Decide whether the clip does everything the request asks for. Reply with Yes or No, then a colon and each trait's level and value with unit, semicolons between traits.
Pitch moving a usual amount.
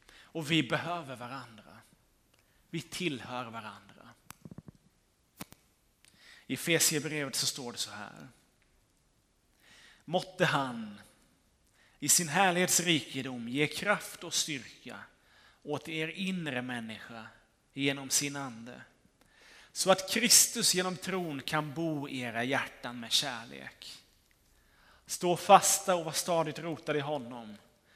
No: wide, 5.8 semitones